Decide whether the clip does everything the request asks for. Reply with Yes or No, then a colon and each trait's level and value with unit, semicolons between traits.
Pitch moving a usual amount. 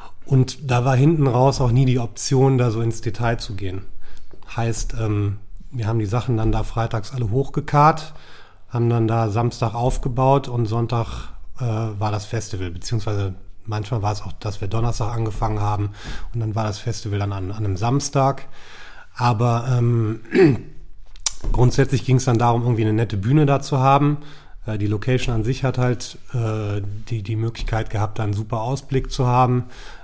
Yes: average, 3.1 semitones